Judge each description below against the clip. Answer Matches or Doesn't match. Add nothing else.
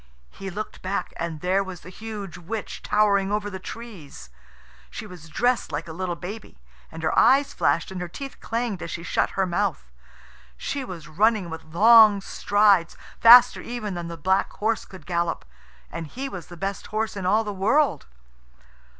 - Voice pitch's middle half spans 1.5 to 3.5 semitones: Doesn't match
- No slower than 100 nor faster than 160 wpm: Doesn't match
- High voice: Matches